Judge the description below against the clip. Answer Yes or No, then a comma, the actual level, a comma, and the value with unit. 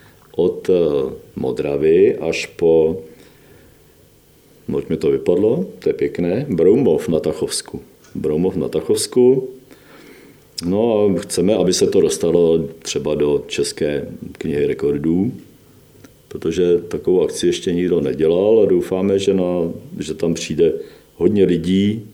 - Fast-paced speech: No, average, 120 wpm